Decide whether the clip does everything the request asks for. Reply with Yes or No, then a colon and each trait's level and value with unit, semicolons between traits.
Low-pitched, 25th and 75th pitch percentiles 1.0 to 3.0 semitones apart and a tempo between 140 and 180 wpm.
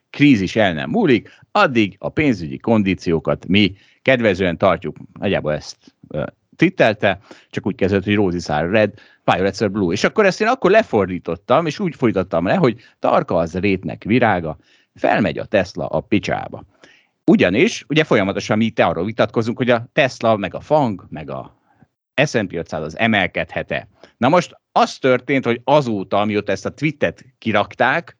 No: low, 105 Hz; average, 4.9 semitones; fast, 155 wpm